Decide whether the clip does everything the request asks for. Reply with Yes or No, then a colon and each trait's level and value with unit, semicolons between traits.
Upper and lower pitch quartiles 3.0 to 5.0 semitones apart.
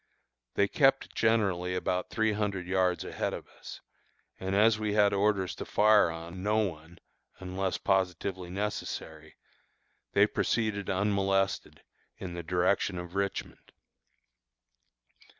No: narrow, 2.4 semitones